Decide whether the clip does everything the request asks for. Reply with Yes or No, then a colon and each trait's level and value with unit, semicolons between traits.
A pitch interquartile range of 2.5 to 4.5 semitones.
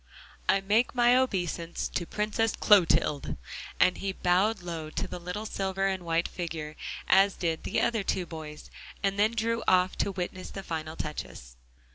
Yes: average, 3.7 semitones